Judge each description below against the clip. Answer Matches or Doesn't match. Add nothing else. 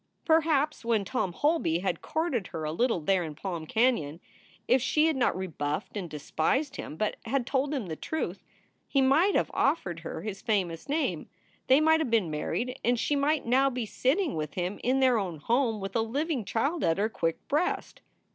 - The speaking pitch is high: Matches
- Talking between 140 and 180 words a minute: Doesn't match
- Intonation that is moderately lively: Doesn't match